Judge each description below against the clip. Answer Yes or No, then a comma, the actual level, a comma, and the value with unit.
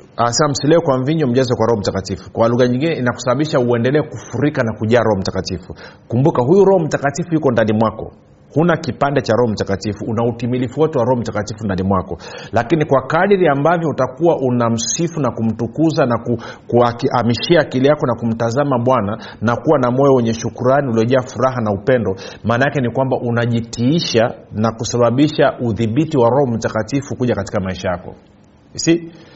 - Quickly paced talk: Yes, fast, 150 wpm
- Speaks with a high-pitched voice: No, low, 120 Hz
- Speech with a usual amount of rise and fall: Yes, average, 3.8 semitones